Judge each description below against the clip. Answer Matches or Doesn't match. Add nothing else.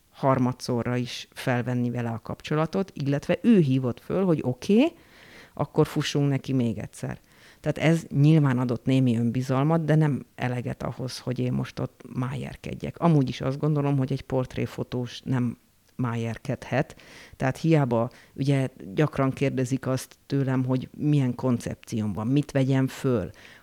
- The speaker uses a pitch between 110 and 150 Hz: Matches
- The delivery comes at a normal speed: Matches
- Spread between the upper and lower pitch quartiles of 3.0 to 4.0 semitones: Doesn't match